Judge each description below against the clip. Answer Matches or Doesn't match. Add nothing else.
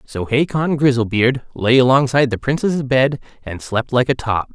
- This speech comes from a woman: Doesn't match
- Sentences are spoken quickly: Doesn't match